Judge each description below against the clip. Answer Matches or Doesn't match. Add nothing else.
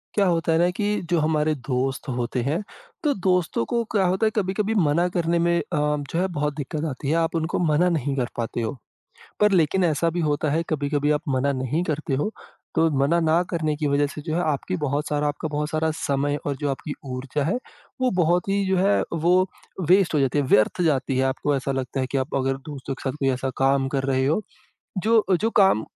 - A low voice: Doesn't match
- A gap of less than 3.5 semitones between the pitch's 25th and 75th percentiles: Doesn't match